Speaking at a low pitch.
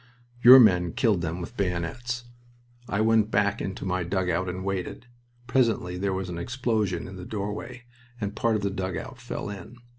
Yes: low, 100 Hz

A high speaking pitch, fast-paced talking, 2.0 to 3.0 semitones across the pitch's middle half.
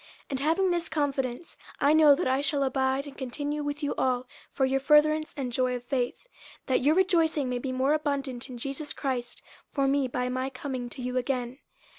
Yes: very high, 270 Hz; fast, 210 wpm; narrow, 2.6 semitones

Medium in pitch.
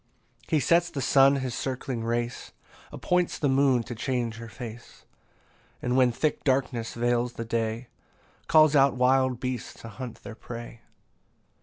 No: low, 125 Hz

